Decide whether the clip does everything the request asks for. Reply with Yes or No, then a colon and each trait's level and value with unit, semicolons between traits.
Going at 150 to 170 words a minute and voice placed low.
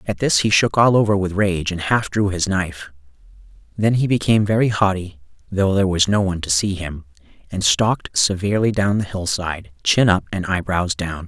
No: average, 195 wpm; very low, 95 Hz